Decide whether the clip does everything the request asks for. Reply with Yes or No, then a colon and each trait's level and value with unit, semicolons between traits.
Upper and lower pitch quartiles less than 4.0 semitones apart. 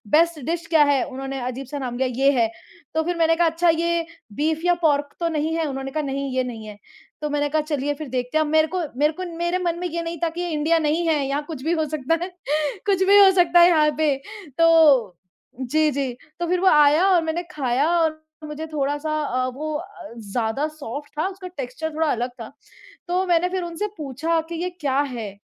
Yes: average, 3.4 semitones